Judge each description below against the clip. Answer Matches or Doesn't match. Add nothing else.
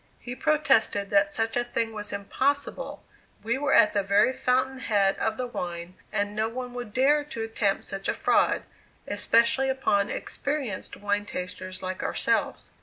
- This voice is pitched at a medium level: Doesn't match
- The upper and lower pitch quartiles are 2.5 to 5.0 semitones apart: Matches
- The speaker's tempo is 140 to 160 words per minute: Doesn't match